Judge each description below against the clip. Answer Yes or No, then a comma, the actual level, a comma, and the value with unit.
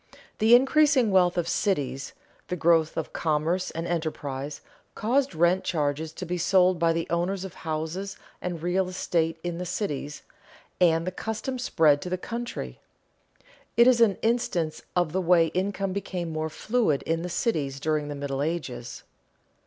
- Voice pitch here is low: No, medium, 175 Hz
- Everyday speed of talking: Yes, average, 160 wpm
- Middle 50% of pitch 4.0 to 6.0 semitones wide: No, average, 3.4 semitones